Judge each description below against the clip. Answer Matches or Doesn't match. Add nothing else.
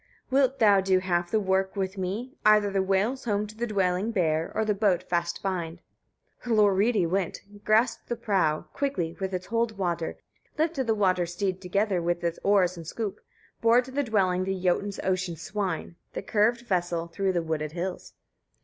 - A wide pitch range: Doesn't match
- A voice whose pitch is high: Matches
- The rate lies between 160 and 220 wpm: Matches